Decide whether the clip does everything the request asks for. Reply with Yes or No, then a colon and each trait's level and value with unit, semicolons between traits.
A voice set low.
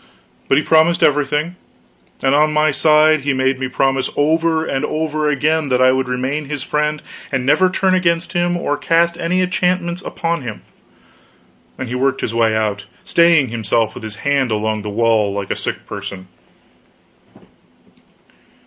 No: medium, 145 Hz